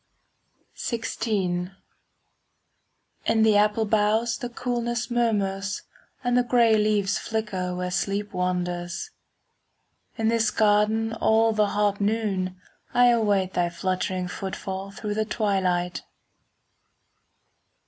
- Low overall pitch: No, high, 210 Hz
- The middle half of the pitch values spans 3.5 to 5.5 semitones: No, average, 3.0 semitones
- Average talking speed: No, slow, 105 wpm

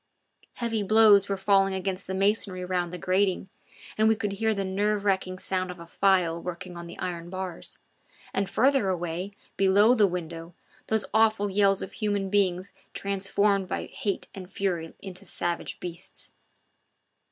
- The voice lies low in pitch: No, high, 195 Hz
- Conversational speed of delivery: Yes, average, 160 wpm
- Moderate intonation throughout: No, narrow, 2.0 semitones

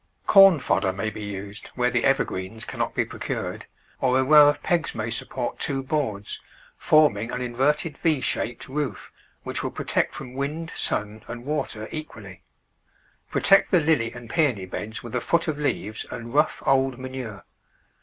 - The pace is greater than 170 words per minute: No, average, 165 wpm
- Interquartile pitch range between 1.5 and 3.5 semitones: No, wide, 5.4 semitones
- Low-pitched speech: Yes, low, 125 Hz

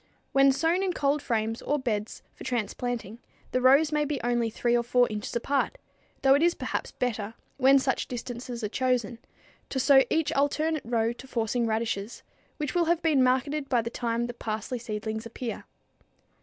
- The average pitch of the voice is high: Yes, high, 245 Hz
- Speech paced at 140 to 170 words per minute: No, average, 180 wpm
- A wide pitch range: No, average, 3.3 semitones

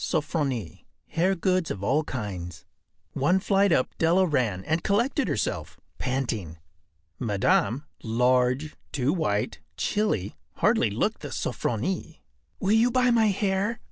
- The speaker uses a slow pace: Yes, slow, 125 wpm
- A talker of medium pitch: Yes, medium, 155 Hz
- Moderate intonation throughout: No, wide, 8.5 semitones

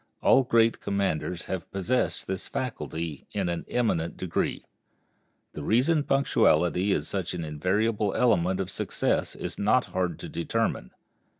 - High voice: No, very low, 95 Hz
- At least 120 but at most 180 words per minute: Yes, slow, 135 wpm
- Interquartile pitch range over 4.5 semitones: Yes, average, 4.9 semitones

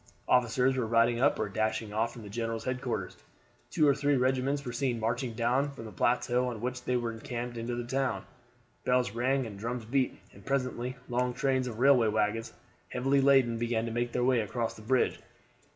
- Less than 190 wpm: No, average, 200 wpm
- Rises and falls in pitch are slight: Yes, narrow, 2.1 semitones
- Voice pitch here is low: Yes, low, 120 Hz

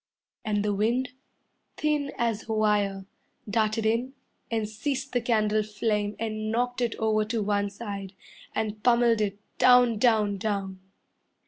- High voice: Yes, high, 215 Hz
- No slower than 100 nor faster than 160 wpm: Yes, average, 140 wpm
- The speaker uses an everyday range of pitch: No, narrow, 2.3 semitones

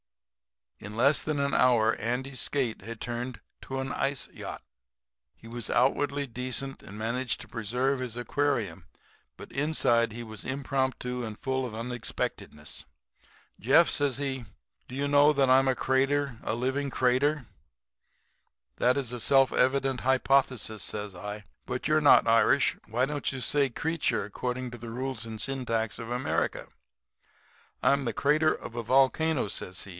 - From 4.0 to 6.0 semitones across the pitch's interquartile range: No, average, 3.0 semitones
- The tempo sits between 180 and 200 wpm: No, average, 155 wpm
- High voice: No, low, 130 Hz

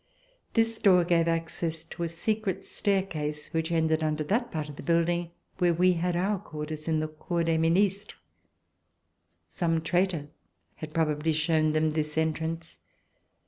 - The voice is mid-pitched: Yes, medium, 165 Hz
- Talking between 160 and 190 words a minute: No, average, 150 wpm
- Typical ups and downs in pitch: No, narrow, 2.3 semitones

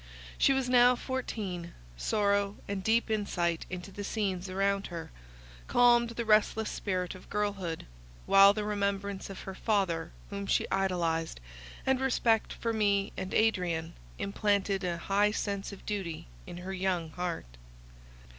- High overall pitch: Yes, high, 200 Hz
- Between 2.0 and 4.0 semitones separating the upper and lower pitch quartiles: Yes, average, 2.7 semitones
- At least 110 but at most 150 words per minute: Yes, average, 145 wpm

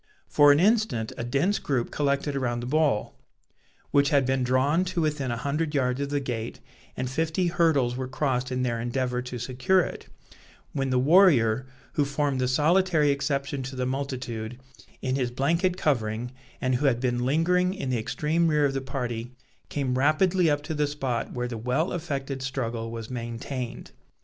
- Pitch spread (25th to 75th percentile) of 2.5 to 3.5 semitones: Yes, average, 3.2 semitones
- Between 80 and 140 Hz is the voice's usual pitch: Yes, low, 135 Hz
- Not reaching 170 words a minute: No, average, 180 wpm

